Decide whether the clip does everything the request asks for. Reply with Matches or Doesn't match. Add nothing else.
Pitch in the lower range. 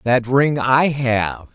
Matches